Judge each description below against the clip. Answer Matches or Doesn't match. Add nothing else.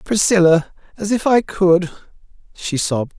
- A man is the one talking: Matches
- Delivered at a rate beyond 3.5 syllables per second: Matches